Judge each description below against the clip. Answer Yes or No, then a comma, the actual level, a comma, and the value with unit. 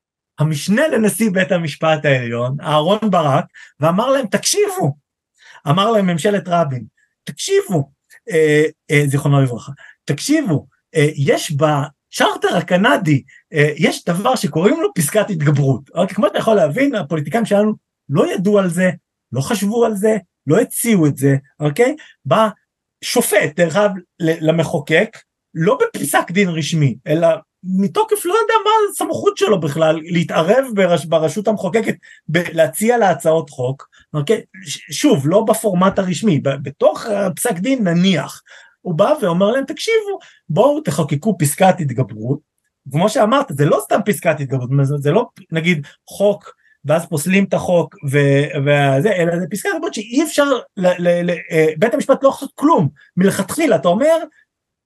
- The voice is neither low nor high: Yes, medium, 180 Hz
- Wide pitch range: Yes, wide, 6.2 semitones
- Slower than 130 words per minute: No, average, 145 wpm